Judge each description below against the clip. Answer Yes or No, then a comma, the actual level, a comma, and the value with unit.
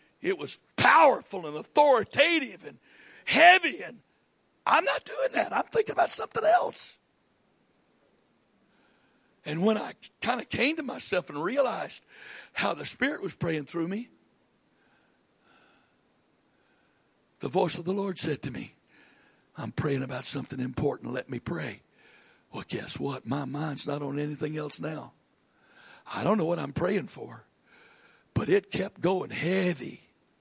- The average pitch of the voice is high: No, medium, 175 Hz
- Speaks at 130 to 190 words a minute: Yes, average, 140 wpm